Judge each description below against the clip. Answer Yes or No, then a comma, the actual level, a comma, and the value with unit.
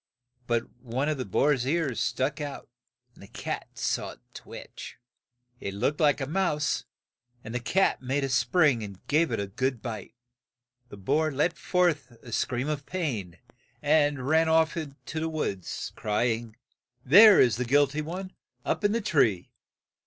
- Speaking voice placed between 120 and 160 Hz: Yes, medium, 140 Hz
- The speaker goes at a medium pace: Yes, average, 170 wpm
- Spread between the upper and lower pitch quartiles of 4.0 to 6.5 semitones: Yes, average, 4.8 semitones